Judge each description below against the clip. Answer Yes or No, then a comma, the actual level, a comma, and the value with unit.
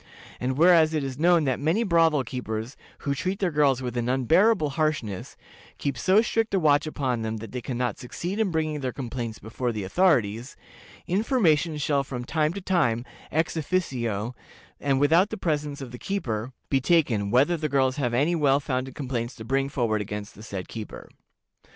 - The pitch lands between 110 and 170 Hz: Yes, medium, 140 Hz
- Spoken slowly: No, average, 190 wpm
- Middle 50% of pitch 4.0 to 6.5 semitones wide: Yes, average, 5.0 semitones